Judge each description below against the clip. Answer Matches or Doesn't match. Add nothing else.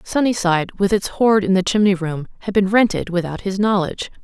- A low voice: Doesn't match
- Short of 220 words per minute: Matches